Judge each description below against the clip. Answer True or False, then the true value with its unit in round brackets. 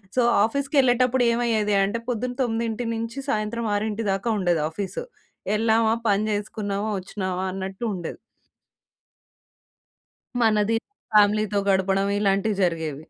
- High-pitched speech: True (210 Hz)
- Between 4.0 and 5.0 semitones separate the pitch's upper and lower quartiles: False (2.8 semitones)